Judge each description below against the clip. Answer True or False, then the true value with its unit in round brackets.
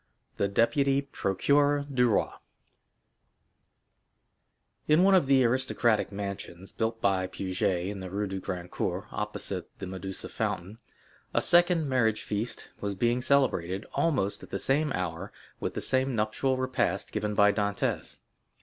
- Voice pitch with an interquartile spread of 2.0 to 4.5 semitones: False (5.6 semitones)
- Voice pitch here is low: True (110 Hz)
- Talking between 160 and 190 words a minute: False (140 wpm)